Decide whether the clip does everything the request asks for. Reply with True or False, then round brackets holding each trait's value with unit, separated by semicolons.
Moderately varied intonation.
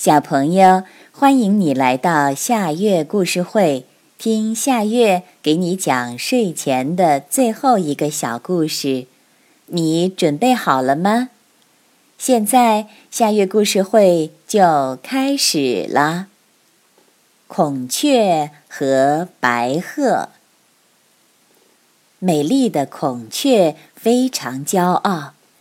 False (7.4 semitones)